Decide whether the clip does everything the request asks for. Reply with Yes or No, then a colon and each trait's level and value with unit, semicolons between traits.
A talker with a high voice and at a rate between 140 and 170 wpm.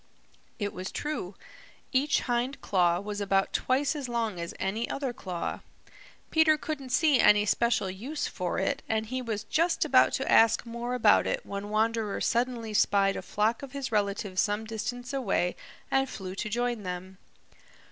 Yes: high, 225 Hz; average, 165 wpm